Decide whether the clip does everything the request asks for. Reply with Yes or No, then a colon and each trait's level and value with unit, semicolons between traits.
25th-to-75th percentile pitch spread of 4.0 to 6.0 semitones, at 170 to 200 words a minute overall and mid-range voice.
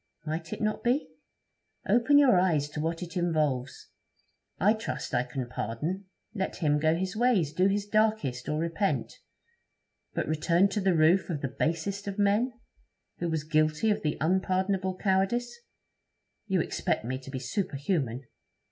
No: average, 4.7 semitones; average, 155 wpm; medium, 175 Hz